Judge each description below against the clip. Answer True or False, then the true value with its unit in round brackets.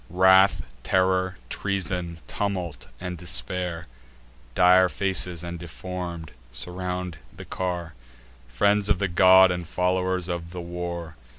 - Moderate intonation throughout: False (1.3 semitones)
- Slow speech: True (115 wpm)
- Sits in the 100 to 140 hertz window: False (90 Hz)